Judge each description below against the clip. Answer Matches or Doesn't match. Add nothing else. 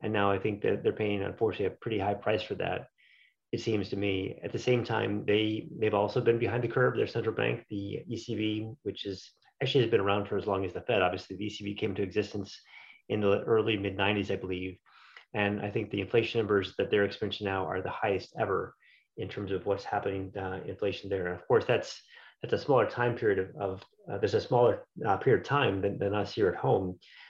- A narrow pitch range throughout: Matches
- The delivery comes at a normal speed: Doesn't match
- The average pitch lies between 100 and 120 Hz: Matches